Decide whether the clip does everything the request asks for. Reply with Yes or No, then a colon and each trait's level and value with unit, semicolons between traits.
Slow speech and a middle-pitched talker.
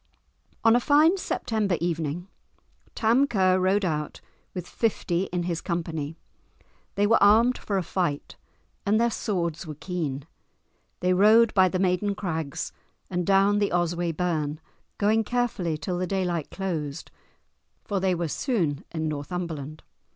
No: average, 145 wpm; medium, 180 Hz